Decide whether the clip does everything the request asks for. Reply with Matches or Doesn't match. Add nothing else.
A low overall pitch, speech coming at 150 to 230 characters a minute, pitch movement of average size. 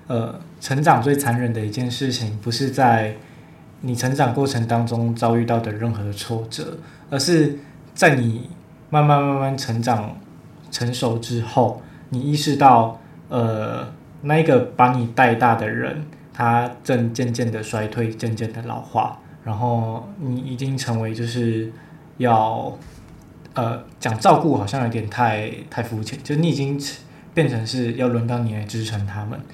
Matches